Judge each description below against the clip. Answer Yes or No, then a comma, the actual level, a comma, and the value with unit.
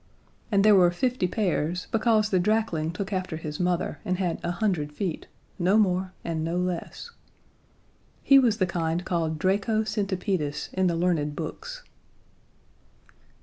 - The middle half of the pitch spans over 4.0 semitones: No, average, 3.7 semitones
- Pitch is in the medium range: Yes, medium, 180 Hz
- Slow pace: No, average, 145 wpm